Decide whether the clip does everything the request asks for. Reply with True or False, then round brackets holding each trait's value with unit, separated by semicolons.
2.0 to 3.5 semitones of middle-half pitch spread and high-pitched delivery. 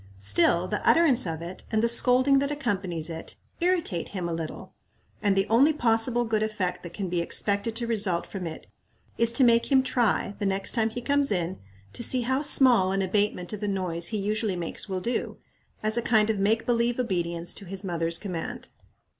False (4.8 semitones; 210 Hz)